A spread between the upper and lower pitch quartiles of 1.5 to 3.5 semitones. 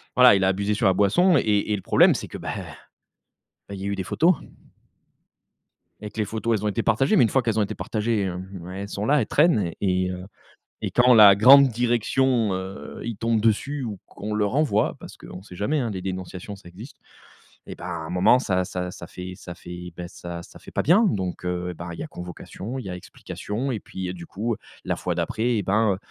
No: average, 4.1 semitones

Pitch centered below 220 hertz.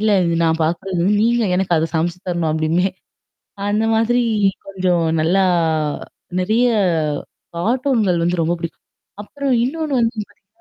Yes: high, 190 Hz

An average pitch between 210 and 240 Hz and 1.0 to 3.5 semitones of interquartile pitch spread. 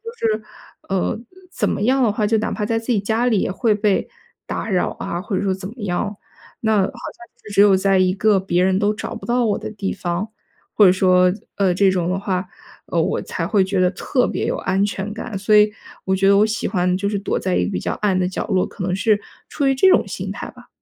No: high, 200 Hz; narrow, 2.5 semitones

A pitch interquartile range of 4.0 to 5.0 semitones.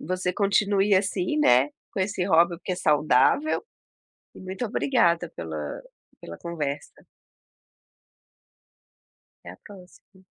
Yes: average, 4.6 semitones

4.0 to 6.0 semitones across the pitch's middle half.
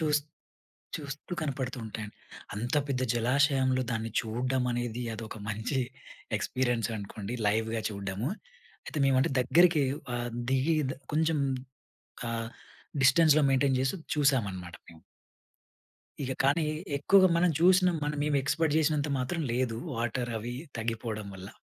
Yes: average, 4.6 semitones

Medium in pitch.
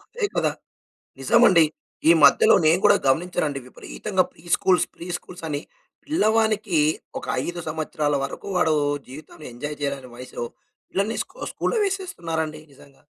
Yes: medium, 165 Hz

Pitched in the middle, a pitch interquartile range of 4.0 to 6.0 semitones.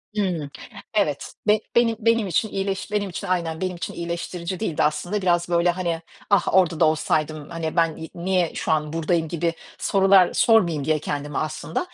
No: medium, 170 Hz; average, 3.2 semitones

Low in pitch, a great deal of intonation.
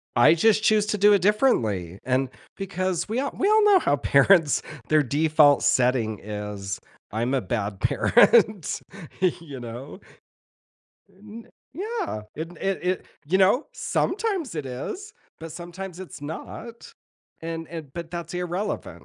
No: medium, 170 Hz; wide, 7.8 semitones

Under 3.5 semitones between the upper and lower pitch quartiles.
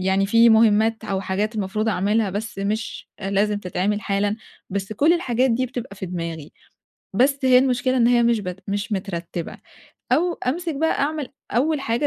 No: average, 4.3 semitones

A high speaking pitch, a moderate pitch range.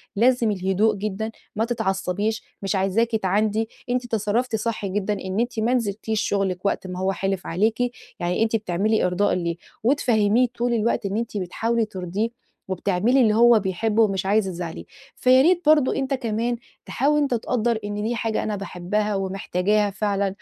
Yes: high, 215 Hz; average, 3.2 semitones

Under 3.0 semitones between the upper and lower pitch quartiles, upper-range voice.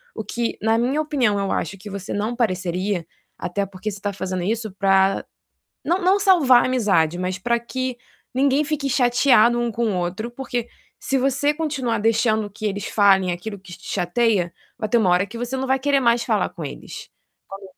No: average, 4.8 semitones; high, 225 Hz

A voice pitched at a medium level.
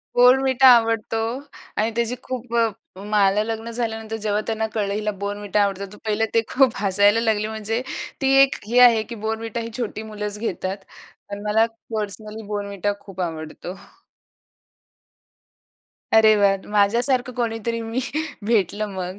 No: high, 220 Hz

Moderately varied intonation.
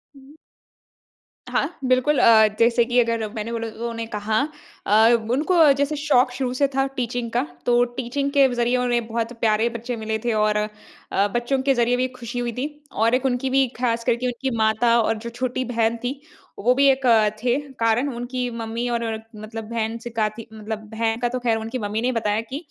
No: narrow, 2.2 semitones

